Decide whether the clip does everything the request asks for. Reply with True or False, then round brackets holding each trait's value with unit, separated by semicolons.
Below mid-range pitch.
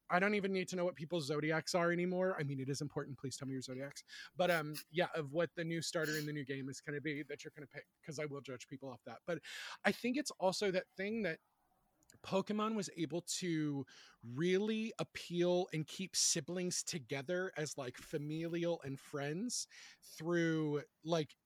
False (160 Hz)